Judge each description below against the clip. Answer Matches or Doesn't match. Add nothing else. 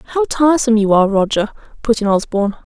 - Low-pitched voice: Doesn't match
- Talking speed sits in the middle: Matches